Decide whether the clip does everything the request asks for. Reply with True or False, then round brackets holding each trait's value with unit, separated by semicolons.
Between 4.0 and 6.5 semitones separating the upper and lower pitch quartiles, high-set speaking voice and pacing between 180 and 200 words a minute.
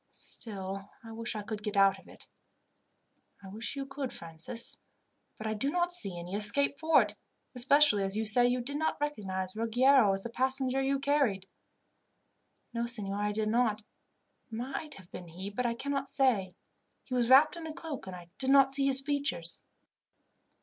True (5.4 semitones; 235 Hz; 185 wpm)